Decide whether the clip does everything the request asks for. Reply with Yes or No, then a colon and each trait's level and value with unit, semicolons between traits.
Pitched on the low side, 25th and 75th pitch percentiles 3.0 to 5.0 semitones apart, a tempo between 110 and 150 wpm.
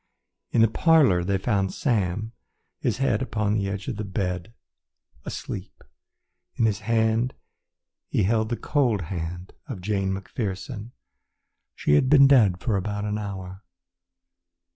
Yes: low, 105 Hz; average, 3.3 semitones; slow, 135 wpm